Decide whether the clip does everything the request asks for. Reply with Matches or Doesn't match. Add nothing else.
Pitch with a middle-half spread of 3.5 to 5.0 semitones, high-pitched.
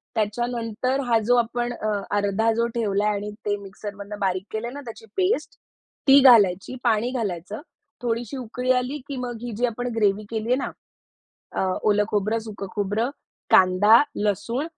Doesn't match